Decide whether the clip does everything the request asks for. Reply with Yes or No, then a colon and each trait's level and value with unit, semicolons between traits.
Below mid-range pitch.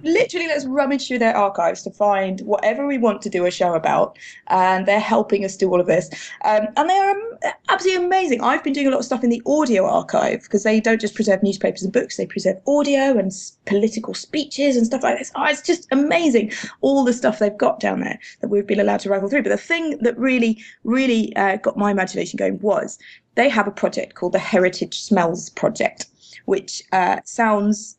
No: high, 225 Hz